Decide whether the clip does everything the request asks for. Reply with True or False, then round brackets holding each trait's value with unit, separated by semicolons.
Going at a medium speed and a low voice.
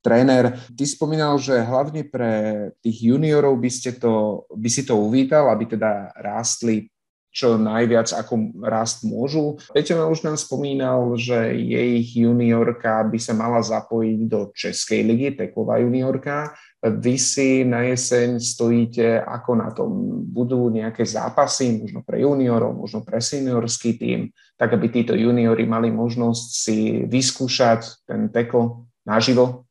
True (140 wpm; 120 Hz)